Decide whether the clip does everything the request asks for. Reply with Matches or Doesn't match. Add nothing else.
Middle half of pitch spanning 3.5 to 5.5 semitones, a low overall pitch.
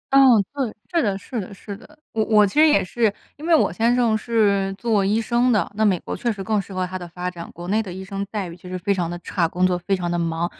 Doesn't match